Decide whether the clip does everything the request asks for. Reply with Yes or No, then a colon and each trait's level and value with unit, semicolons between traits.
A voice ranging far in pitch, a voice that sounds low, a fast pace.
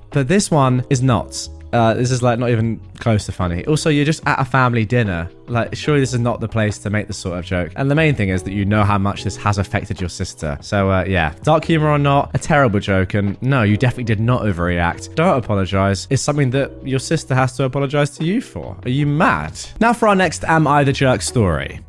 Yes: wide, 6.0 semitones; low, 115 Hz; fast, 250 wpm